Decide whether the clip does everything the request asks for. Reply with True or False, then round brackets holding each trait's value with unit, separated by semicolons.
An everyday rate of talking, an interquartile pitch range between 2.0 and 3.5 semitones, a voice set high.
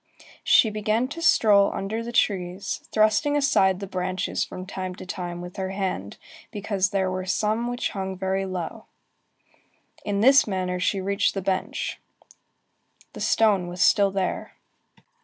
True (155 wpm; 2.5 semitones; 195 Hz)